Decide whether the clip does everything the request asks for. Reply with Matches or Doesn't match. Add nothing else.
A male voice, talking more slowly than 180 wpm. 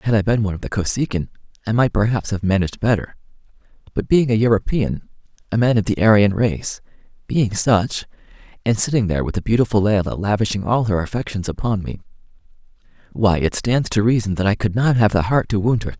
Doesn't match